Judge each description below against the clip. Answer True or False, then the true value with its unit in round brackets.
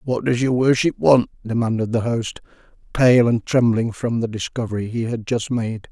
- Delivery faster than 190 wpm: False (185 wpm)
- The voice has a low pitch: True (115 Hz)